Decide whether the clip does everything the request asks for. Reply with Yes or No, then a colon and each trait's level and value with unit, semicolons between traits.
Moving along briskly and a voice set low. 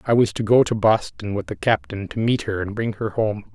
Yes: fast, 270 wpm; low, 110 Hz